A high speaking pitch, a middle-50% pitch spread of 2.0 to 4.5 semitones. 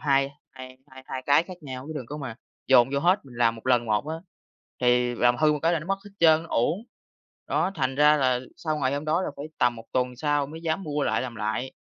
No: medium, 140 Hz; average, 3.8 semitones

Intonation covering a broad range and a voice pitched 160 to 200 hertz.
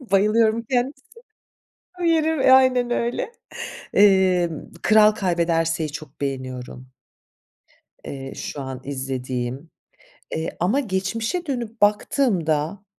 Yes: wide, 8.4 semitones; high, 190 Hz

